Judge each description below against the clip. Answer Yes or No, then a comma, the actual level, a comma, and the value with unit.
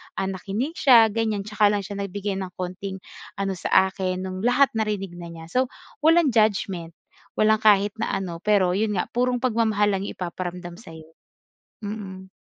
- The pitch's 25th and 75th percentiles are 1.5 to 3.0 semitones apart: Yes, average, 2.7 semitones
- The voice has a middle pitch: No, high, 200 Hz